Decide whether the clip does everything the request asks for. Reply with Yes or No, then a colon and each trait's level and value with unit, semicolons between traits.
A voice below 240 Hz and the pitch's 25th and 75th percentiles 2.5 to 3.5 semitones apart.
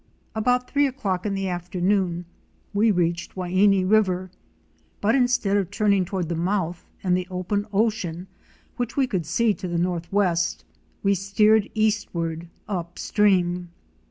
Yes: high, 190 Hz; average, 3.0 semitones